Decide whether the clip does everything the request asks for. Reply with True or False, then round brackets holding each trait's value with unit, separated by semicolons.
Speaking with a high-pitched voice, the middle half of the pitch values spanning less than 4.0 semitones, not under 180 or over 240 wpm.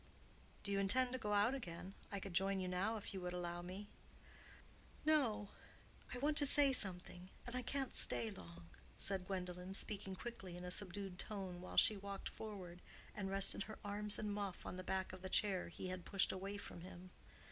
True (195 Hz; 2.5 semitones; 200 wpm)